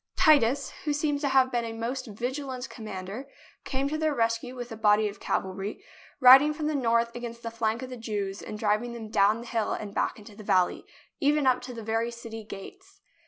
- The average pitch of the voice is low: No, high, 235 Hz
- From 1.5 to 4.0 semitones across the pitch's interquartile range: Yes, average, 3.5 semitones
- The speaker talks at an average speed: No, fast, 210 wpm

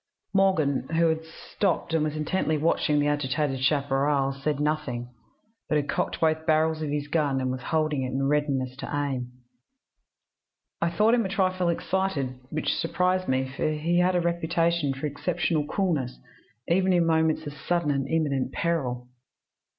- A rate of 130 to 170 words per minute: Yes, average, 165 wpm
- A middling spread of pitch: Yes, average, 3.5 semitones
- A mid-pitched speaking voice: Yes, medium, 155 Hz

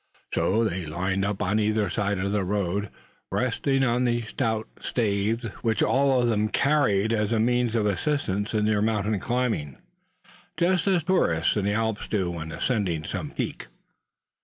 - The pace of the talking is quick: No, average, 165 wpm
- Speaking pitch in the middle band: No, low, 110 Hz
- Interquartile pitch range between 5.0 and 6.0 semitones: No, average, 3.3 semitones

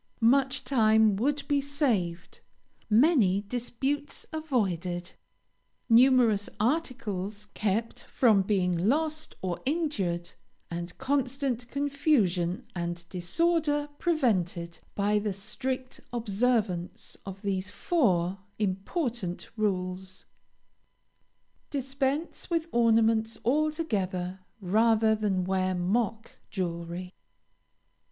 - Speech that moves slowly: Yes, slow, 85 wpm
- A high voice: Yes, high, 220 Hz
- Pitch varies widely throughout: Yes, wide, 6.3 semitones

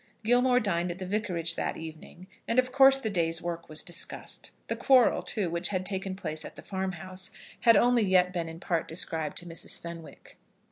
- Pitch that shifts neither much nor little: Yes, average, 4.1 semitones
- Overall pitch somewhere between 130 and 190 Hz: Yes, medium, 185 Hz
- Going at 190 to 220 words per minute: Yes, average, 195 wpm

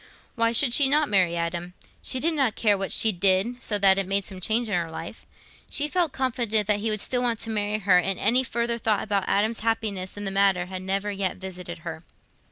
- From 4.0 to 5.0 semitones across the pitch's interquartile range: No, average, 3.5 semitones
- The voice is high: Yes, high, 205 Hz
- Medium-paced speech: No, fast, 230 wpm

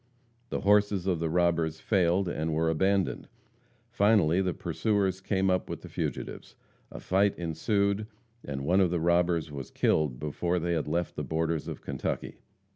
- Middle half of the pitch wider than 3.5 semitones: No, average, 3.2 semitones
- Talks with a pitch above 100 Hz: No, very low, 85 Hz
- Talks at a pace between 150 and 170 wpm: Yes, average, 165 wpm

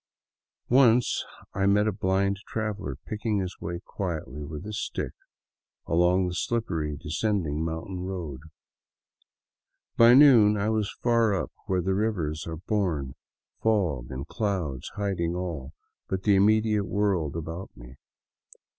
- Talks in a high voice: No, very low, 95 Hz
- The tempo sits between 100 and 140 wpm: Yes, slow, 135 wpm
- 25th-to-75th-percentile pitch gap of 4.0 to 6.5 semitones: Yes, average, 4.6 semitones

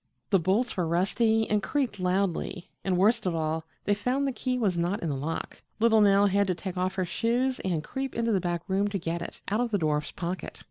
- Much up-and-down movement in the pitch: No, average, 4.3 semitones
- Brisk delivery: Yes, fast, 235 wpm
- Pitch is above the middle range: Yes, high, 195 Hz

